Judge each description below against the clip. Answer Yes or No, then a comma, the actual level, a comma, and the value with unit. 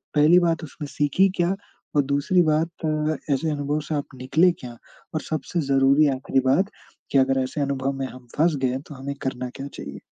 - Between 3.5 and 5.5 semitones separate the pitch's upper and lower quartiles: No, average, 2.8 semitones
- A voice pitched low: No, medium, 145 Hz